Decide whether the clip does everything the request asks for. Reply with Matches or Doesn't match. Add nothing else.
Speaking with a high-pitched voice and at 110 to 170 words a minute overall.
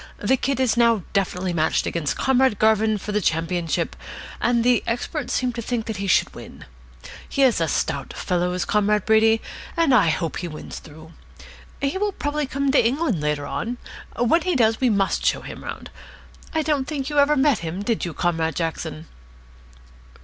Doesn't match